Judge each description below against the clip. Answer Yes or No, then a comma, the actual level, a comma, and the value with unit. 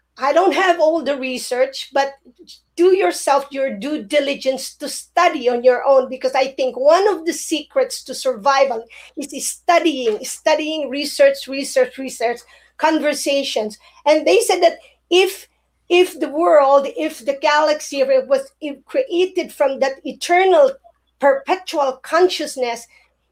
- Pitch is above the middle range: Yes, very high, 285 Hz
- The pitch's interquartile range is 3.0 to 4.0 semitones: Yes, average, 3.7 semitones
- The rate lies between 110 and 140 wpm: Yes, slow, 135 wpm